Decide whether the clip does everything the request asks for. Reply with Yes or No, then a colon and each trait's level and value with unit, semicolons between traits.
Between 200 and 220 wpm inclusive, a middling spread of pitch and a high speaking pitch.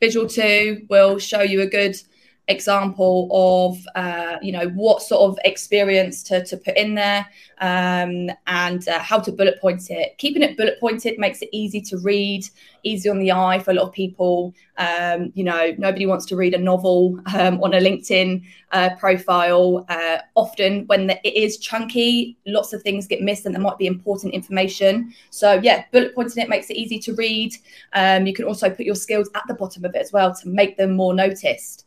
No: fast, 205 wpm; narrow, 2.3 semitones; high, 195 Hz